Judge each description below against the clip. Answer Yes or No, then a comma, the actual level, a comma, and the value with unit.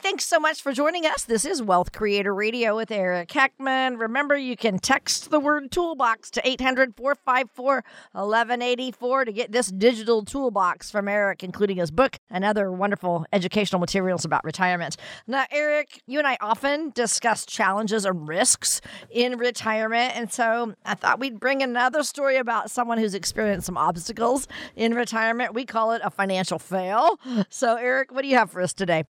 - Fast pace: No, average, 175 wpm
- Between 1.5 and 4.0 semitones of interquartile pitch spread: No, average, 4.7 semitones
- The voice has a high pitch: Yes, high, 230 Hz